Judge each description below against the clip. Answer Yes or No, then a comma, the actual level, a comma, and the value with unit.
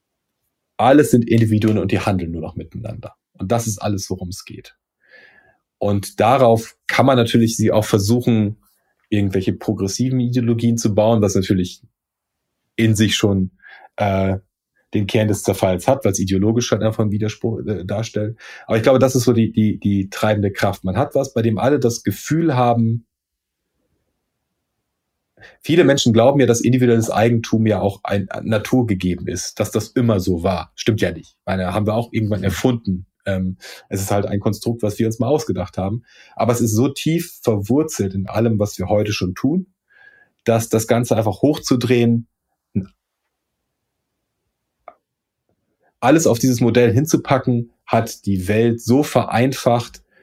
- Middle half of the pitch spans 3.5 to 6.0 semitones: No, average, 3.0 semitones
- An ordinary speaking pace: Yes, average, 160 wpm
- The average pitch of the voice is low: Yes, low, 110 Hz